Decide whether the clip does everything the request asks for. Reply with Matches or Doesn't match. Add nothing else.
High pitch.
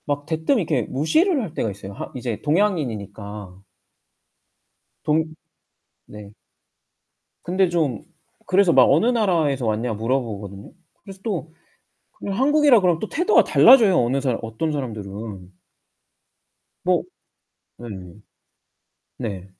Doesn't match